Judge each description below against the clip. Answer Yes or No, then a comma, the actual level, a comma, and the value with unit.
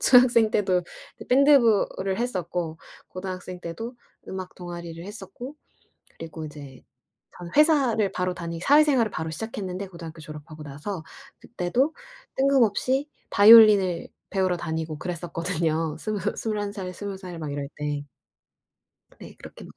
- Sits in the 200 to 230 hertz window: No, medium, 185 Hz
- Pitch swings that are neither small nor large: Yes, average, 5.0 semitones